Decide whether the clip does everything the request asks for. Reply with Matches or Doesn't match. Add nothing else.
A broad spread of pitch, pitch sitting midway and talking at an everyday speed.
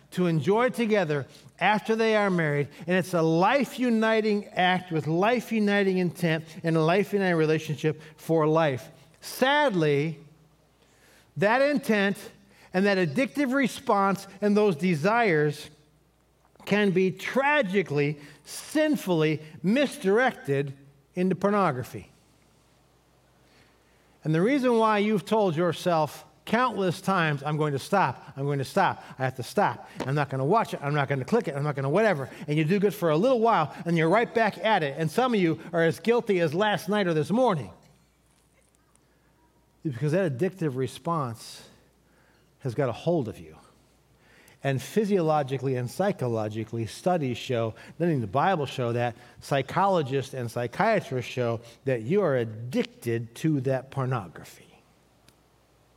Matches